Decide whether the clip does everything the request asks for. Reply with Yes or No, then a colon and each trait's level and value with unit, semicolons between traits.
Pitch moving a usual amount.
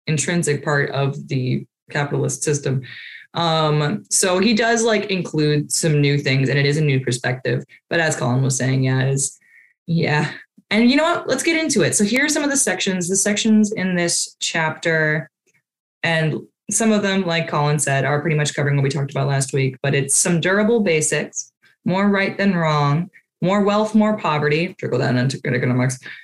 No: wide, 5.8 semitones